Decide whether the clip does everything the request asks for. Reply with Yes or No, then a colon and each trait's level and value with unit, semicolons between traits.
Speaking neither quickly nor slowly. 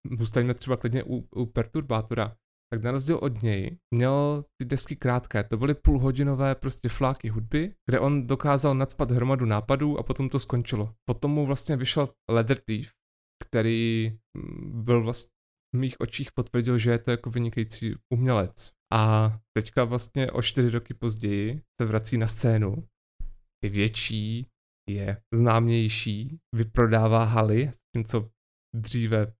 Yes: average, 145 wpm